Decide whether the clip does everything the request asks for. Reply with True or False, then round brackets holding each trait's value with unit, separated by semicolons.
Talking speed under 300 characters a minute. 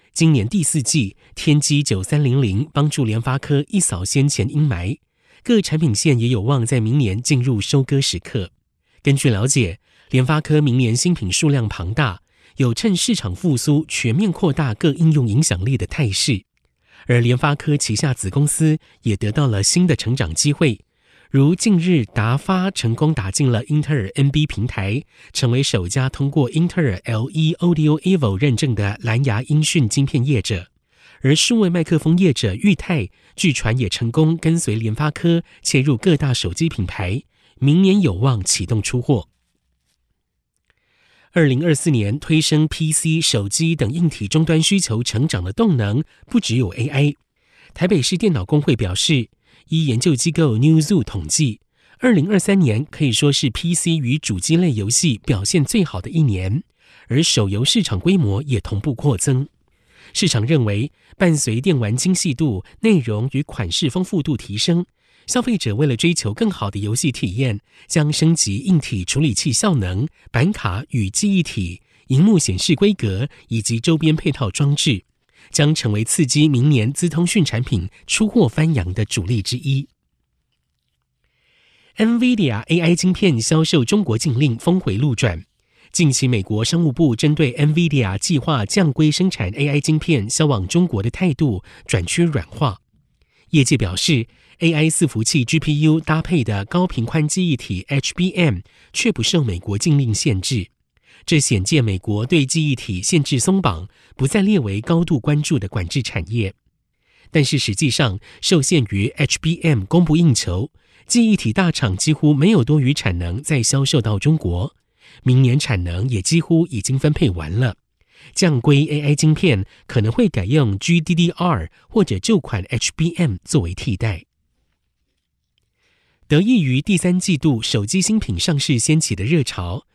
True (255 characters per minute)